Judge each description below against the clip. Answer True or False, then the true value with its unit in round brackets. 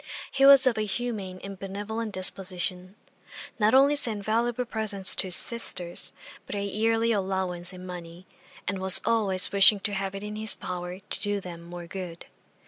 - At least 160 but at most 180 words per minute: True (175 wpm)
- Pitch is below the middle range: False (195 Hz)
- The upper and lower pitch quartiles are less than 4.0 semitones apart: True (3.1 semitones)